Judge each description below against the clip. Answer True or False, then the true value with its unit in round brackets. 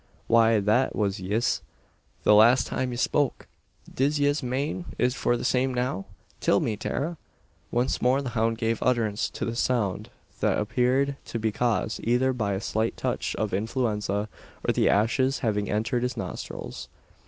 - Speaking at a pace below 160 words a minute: False (165 wpm)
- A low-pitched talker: True (120 Hz)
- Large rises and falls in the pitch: False (3.1 semitones)